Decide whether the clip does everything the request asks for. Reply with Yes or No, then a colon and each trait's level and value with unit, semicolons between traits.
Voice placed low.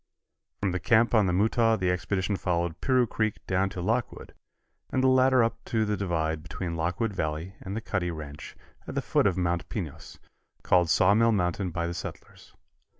Yes: very low, 95 Hz